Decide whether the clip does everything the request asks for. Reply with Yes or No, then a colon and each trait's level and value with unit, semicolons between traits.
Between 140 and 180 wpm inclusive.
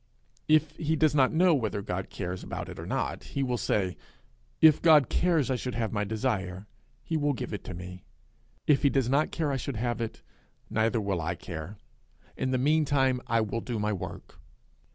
No: average, 195 wpm